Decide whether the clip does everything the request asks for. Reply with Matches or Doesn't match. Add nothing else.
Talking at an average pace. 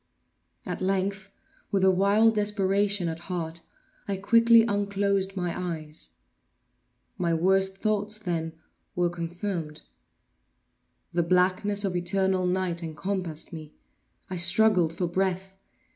Doesn't match